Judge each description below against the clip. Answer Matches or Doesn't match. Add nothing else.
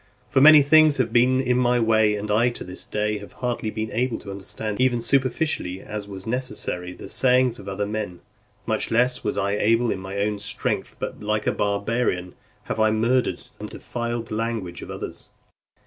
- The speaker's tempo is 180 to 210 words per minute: Matches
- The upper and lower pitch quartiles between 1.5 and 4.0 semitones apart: Matches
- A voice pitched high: Doesn't match